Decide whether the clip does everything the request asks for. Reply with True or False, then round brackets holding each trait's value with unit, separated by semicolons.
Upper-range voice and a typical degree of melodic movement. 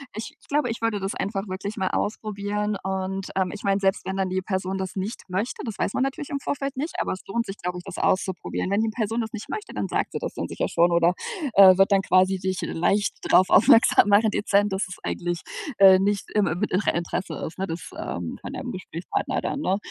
False (195 Hz; 2.3 semitones)